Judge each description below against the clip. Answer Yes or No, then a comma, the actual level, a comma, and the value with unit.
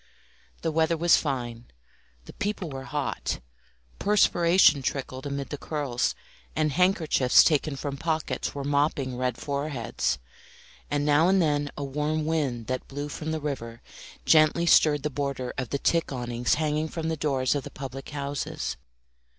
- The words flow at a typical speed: Yes, average, 155 wpm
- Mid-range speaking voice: Yes, medium, 145 Hz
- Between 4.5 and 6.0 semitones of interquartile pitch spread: No, average, 2.8 semitones